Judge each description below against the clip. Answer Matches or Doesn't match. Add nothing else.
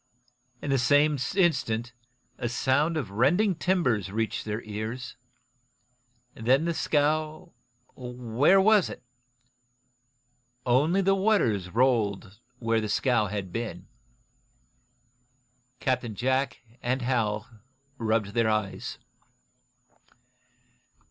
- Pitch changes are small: Doesn't match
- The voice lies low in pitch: Matches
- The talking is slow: Matches